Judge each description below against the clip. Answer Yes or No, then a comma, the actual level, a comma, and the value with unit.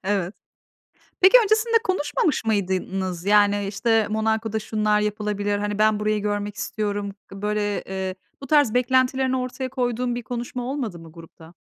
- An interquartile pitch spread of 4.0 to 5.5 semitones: No, average, 3.3 semitones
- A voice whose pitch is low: No, high, 210 Hz